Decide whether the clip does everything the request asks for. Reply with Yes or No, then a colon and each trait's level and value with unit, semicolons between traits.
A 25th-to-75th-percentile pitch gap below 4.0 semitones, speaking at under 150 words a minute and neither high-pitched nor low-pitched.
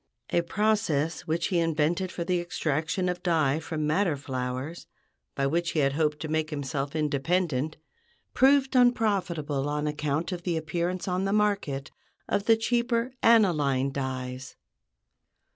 No: average, 4.3 semitones; average, 140 wpm; medium, 160 Hz